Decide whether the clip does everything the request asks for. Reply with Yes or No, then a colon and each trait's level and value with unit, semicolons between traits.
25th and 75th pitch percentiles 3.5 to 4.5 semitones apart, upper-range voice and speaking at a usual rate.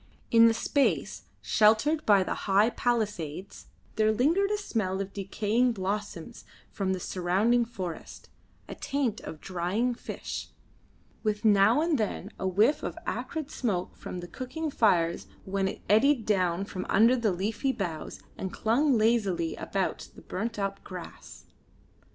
Yes: average, 4.0 semitones; high, 210 Hz; average, 145 wpm